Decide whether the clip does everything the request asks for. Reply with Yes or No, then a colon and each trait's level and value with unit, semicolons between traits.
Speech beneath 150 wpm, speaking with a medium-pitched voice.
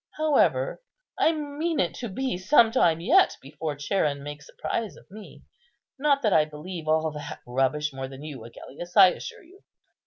No: average, 180 wpm; medium, 175 Hz